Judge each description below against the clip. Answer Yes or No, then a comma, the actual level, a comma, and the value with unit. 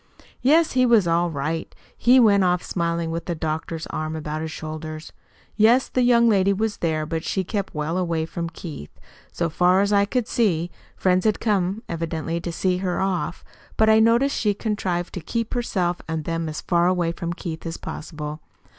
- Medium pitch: Yes, medium, 175 Hz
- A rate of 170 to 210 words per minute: Yes, average, 190 wpm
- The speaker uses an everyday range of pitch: Yes, average, 4.2 semitones